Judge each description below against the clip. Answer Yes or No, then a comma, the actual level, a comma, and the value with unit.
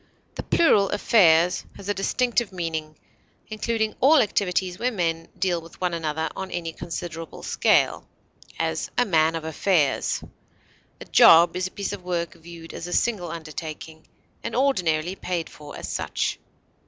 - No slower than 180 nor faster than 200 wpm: No, average, 155 wpm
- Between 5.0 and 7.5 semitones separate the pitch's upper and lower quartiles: No, average, 3.6 semitones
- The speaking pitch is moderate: Yes, medium, 175 Hz